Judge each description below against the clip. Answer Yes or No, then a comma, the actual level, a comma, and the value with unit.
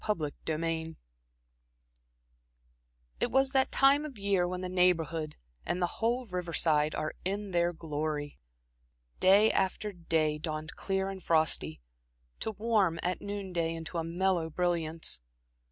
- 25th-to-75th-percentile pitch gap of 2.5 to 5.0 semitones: Yes, average, 3.4 semitones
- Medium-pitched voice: Yes, medium, 175 Hz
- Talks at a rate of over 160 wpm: No, slow, 135 wpm